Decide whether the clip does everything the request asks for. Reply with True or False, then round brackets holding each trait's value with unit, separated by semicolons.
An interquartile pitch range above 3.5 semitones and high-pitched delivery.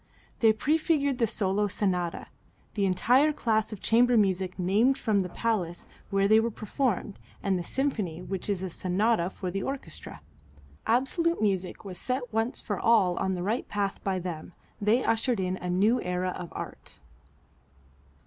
True (4.1 semitones; 205 Hz)